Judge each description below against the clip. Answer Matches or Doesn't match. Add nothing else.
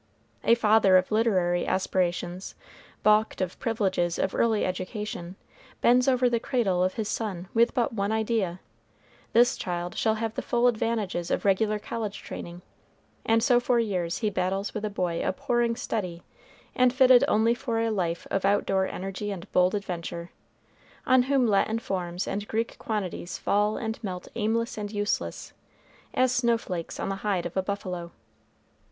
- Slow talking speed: Doesn't match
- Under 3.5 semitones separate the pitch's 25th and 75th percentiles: Doesn't match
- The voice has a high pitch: Matches